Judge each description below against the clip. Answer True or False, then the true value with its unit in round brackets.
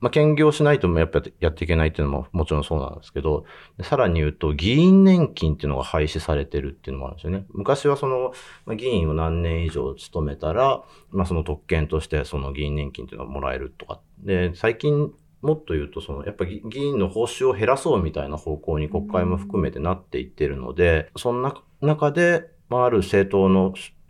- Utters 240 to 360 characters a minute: False (430 characters per minute)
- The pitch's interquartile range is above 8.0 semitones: True (8.5 semitones)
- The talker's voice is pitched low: True (90 Hz)